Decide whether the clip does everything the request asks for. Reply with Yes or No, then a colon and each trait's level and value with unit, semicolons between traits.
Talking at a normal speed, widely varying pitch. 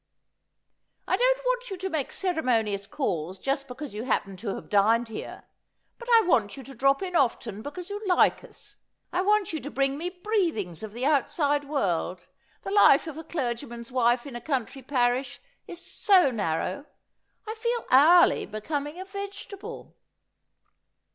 Yes: average, 170 wpm; wide, 7.6 semitones